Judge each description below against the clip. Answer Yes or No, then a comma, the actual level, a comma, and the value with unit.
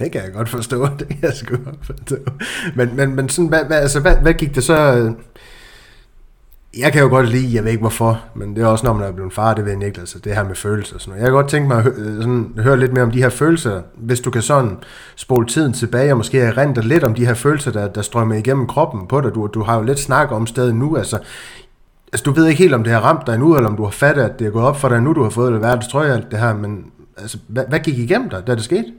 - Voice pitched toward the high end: No, low, 125 Hz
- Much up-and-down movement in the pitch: No, average, 3.8 semitones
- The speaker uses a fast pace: Yes, fast, 305 wpm